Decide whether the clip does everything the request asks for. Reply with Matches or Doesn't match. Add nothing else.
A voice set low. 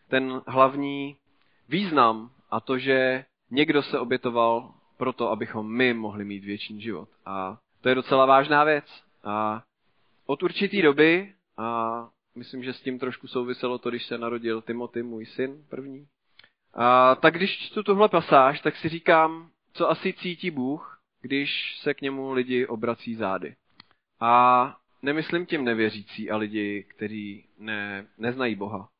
Matches